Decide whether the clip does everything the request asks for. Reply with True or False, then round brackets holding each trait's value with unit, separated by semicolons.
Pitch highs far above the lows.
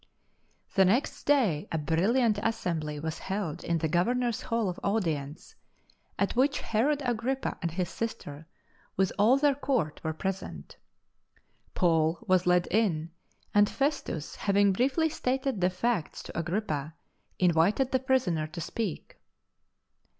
True (6.7 semitones)